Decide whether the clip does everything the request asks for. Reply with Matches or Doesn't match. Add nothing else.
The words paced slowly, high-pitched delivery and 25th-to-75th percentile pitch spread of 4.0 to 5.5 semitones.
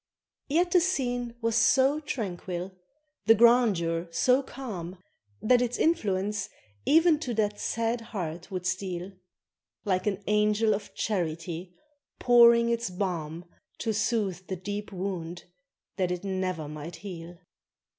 Matches